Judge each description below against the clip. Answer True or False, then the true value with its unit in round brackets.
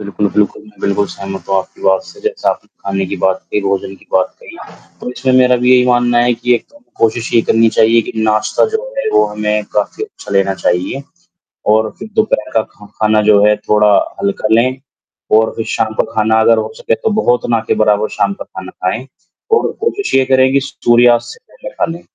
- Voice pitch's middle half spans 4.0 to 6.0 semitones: False (3.4 semitones)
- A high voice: False (110 Hz)